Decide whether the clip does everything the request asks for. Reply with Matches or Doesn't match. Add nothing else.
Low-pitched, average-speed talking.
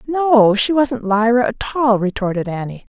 Doesn't match